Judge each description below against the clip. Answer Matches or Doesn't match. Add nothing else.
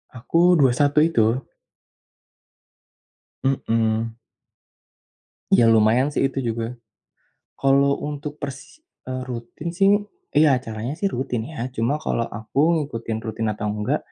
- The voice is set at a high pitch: Doesn't match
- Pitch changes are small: Doesn't match